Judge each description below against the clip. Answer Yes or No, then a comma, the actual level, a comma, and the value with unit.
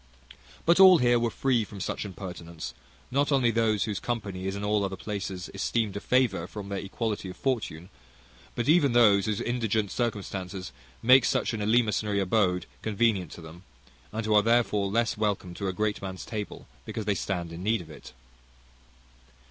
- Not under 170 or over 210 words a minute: Yes, average, 180 wpm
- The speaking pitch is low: Yes, low, 105 Hz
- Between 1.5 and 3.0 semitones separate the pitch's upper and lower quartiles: No, average, 3.4 semitones